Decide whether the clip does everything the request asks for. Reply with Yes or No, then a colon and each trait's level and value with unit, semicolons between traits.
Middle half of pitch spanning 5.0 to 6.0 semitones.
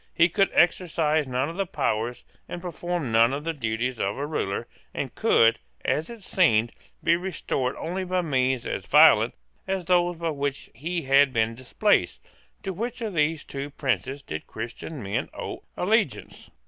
Yes: wide, 5.6 semitones